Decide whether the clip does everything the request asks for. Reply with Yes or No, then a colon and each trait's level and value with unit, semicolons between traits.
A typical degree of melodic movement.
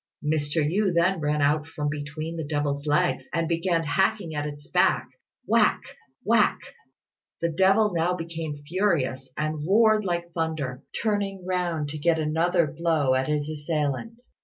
Yes: average, 3.3 semitones